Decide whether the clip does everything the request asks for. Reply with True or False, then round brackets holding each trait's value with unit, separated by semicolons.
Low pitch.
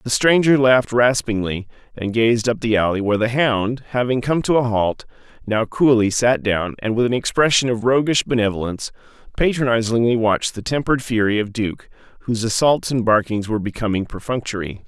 True (115 Hz)